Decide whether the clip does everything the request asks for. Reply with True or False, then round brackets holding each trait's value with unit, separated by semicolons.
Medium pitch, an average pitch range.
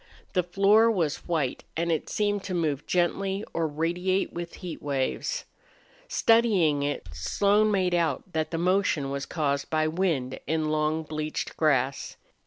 True (165 Hz; 3.9 semitones)